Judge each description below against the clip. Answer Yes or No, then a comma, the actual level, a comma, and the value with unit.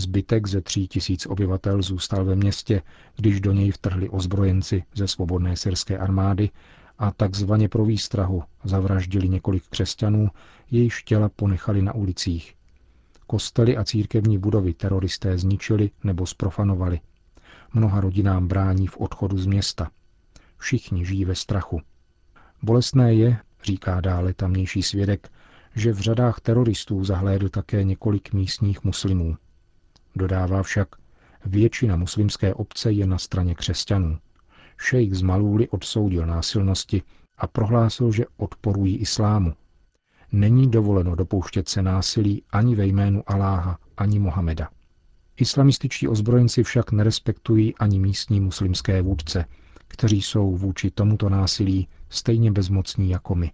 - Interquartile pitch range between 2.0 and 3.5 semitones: Yes, narrow, 2.4 semitones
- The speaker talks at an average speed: Yes, average, 125 wpm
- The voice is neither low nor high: No, low, 100 Hz